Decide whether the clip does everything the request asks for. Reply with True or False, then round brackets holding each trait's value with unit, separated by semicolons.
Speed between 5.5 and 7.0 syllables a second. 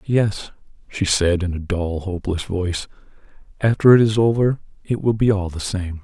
False (5.0 syllables/s)